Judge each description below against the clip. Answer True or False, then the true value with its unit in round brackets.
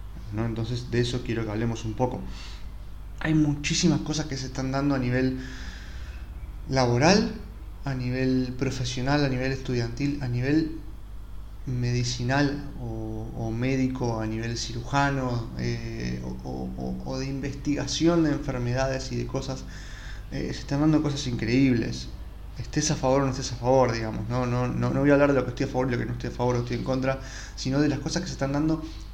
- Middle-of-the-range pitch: False (125 Hz)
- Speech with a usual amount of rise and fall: True (3.4 semitones)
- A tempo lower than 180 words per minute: False (190 wpm)